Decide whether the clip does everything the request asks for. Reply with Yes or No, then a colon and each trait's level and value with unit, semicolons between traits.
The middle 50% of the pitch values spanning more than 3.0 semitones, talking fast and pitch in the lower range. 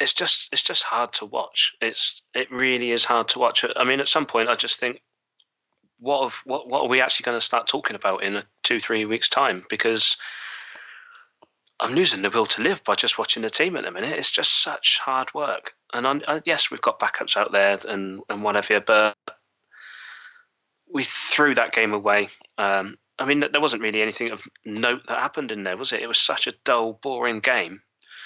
Yes: average, 4.1 semitones; fast, 210 wpm; low, 110 Hz